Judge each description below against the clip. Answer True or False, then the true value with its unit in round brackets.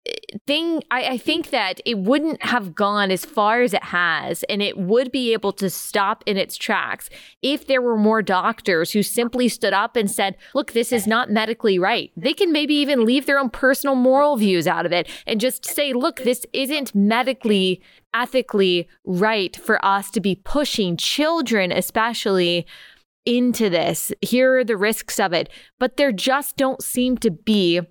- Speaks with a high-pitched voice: True (230 Hz)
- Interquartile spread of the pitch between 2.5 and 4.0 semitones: False (4.8 semitones)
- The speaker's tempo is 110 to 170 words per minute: False (185 wpm)